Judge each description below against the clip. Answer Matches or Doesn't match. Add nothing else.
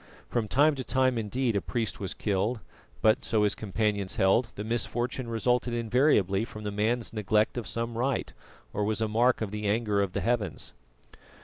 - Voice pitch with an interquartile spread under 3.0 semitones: Matches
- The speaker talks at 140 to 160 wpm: Doesn't match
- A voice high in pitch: Doesn't match